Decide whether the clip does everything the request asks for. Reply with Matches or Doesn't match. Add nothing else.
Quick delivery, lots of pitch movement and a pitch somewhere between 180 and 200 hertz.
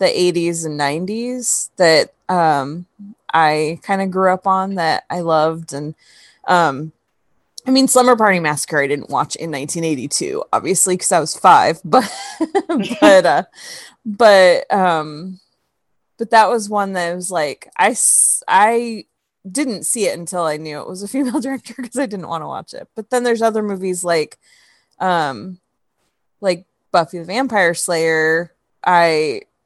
Doesn't match